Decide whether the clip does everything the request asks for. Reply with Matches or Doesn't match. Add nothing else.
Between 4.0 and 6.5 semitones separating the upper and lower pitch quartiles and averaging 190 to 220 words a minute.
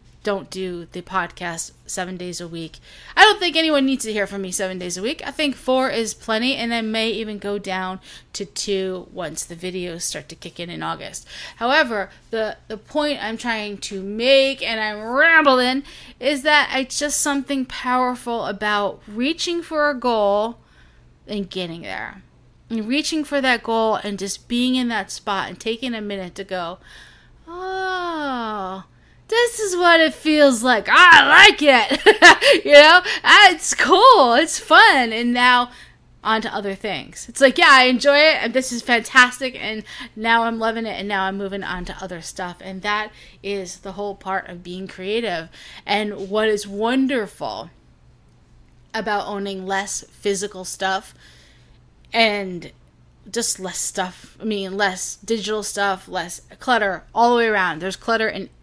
Doesn't match